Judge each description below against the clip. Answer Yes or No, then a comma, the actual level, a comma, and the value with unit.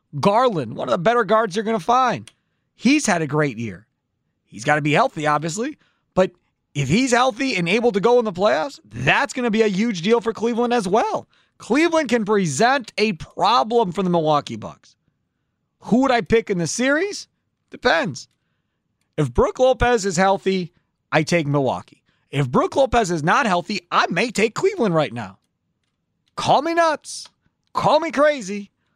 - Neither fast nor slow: Yes, average, 180 wpm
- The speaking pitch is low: No, high, 215 Hz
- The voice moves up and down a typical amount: No, wide, 6.5 semitones